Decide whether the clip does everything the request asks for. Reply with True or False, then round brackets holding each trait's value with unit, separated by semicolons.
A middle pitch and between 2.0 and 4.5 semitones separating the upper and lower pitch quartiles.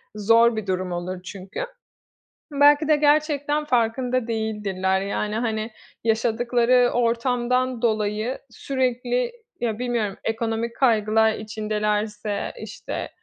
False (225 Hz; 2.8 semitones)